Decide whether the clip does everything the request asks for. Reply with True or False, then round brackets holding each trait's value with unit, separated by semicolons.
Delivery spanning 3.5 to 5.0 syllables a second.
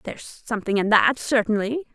False (5.8 syllables/s)